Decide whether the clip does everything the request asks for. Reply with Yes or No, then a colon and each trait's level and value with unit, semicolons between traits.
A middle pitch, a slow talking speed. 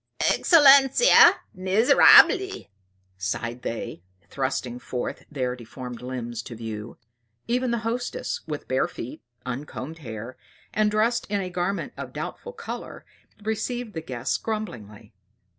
Yes: medium, 150 Hz; slow, 120 wpm